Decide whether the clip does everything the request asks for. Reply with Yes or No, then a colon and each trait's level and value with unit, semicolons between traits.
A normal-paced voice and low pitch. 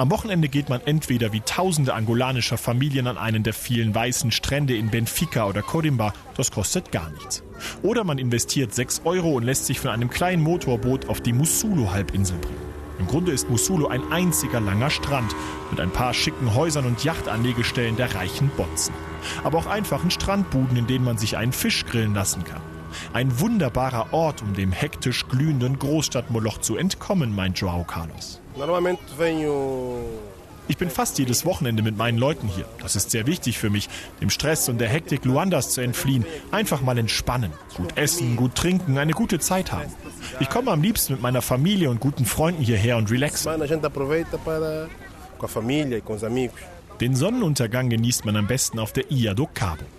Yes: average, 165 wpm; low, 125 Hz